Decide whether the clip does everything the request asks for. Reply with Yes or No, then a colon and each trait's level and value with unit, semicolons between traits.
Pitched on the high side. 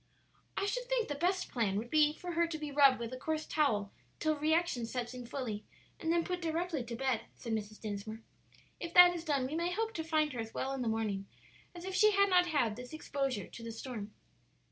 Yes: very high, 285 Hz